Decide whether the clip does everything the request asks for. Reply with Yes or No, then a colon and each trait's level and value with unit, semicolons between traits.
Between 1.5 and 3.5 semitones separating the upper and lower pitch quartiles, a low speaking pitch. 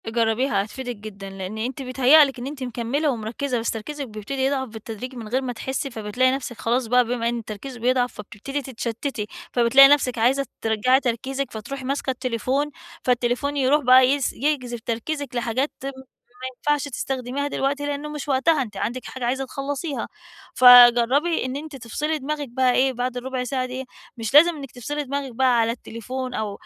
No: average, 2.8 semitones; very high, 255 Hz